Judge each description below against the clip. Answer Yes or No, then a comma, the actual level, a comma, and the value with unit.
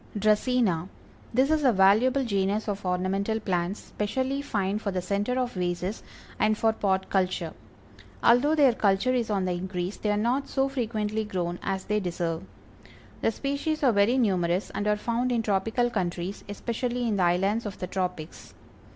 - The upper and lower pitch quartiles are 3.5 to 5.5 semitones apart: Yes, average, 4.3 semitones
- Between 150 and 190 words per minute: Yes, average, 170 wpm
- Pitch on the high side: Yes, high, 210 Hz